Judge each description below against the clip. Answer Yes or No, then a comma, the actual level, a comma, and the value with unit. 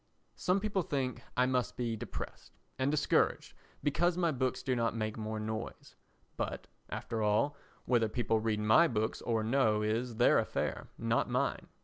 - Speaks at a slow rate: No, average, 160 wpm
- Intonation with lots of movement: No, average, 3.9 semitones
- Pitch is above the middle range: No, low, 120 Hz